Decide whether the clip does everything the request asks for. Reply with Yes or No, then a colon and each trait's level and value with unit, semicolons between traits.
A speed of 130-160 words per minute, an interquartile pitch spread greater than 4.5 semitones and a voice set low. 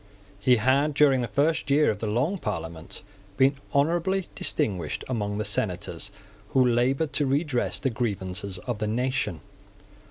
Yes: average, 150 wpm; average, 5.2 semitones; low, 125 Hz